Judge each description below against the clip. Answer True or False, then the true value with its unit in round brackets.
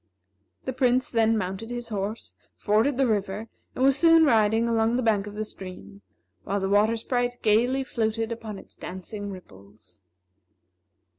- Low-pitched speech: False (220 Hz)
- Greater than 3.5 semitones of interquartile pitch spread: False (3.1 semitones)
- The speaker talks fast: False (155 wpm)